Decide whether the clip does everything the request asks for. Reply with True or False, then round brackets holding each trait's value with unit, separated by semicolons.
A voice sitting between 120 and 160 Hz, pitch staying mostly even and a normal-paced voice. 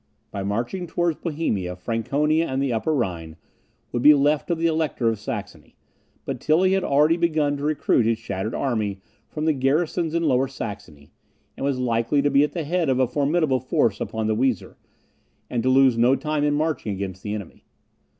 False (135 Hz; 5.5 semitones; 190 wpm)